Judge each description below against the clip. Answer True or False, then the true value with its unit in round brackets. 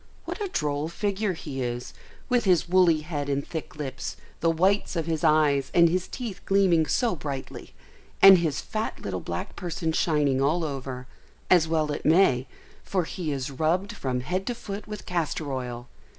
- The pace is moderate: True (180 wpm)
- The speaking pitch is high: False (160 Hz)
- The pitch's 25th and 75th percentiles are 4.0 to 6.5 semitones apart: True (4.6 semitones)